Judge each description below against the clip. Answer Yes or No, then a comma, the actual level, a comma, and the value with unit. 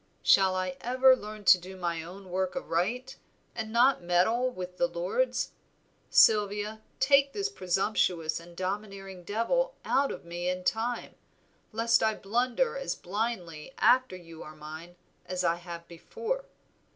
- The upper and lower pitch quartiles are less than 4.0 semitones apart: No, wide, 5.5 semitones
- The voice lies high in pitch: Yes, high, 195 Hz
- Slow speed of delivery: No, average, 145 wpm